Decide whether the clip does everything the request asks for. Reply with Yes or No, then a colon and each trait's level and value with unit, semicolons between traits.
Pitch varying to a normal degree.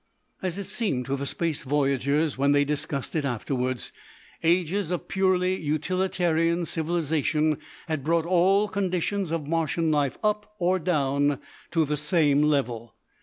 Yes: average, 4.0 semitones